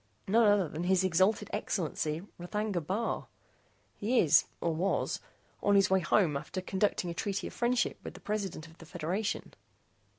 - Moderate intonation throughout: Yes, average, 3.6 semitones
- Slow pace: No, average, 165 wpm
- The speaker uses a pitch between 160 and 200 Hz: Yes, high, 190 Hz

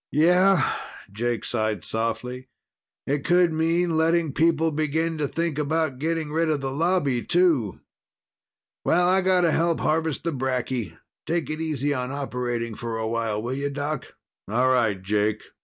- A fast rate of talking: No, average, 155 wpm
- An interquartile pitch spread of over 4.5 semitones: Yes, average, 4.9 semitones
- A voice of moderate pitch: Yes, medium, 145 Hz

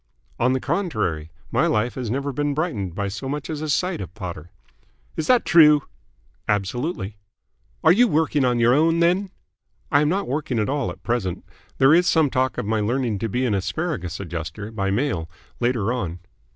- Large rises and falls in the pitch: Yes, wide, 6.8 semitones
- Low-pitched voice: Yes, low, 125 Hz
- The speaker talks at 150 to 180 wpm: No, average, 190 wpm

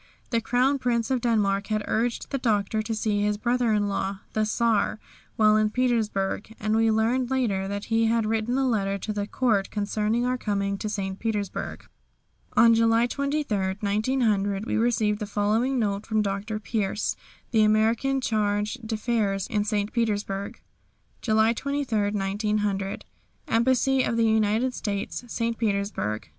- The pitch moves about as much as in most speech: No, narrow, 2.3 semitones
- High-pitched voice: Yes, high, 215 Hz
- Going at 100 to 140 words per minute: No, average, 155 wpm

